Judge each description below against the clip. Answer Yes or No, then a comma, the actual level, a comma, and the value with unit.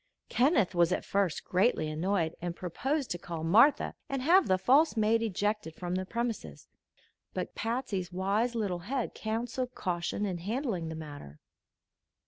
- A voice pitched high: Yes, high, 200 Hz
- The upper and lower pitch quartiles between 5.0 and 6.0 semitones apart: Yes, wide, 5.4 semitones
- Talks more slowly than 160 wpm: Yes, average, 150 wpm